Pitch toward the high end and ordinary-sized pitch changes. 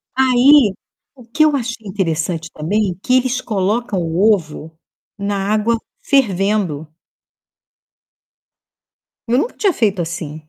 No: high, 205 Hz; wide, 6.0 semitones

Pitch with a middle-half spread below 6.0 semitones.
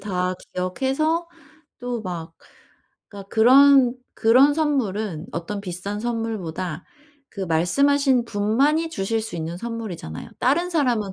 No: wide, 6.5 semitones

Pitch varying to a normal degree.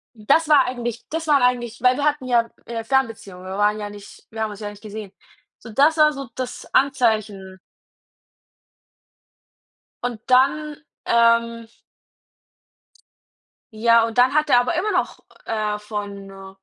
Yes: average, 4.2 semitones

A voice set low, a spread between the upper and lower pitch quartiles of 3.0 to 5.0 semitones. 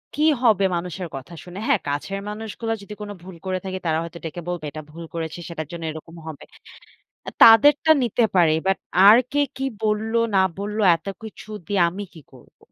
No: high, 190 Hz; average, 4.4 semitones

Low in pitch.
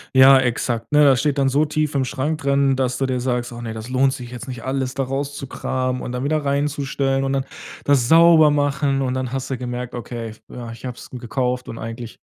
Yes: low, 130 Hz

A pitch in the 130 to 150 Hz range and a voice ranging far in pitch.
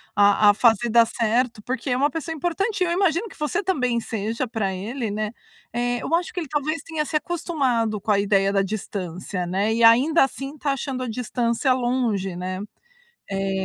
No: high, 240 Hz; wide, 6.0 semitones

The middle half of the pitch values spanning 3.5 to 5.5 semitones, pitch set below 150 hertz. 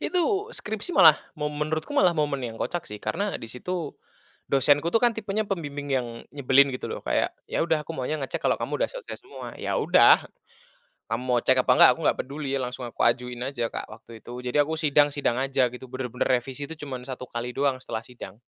Yes: average, 4.2 semitones; medium, 140 Hz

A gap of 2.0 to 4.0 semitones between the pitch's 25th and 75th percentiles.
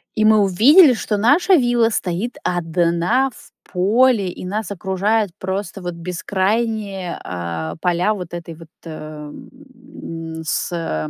No: average, 4.9 semitones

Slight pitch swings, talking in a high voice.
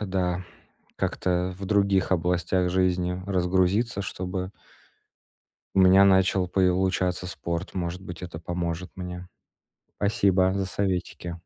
No: narrow, 1.1 semitones; very low, 90 Hz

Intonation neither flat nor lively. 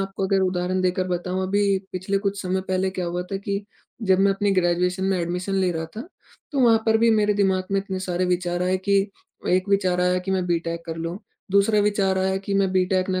No: narrow, 1.6 semitones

